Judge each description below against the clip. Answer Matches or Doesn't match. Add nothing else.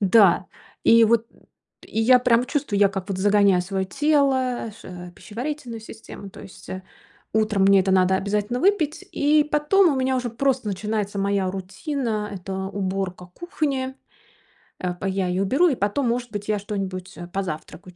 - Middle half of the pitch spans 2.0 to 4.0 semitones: Doesn't match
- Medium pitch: Doesn't match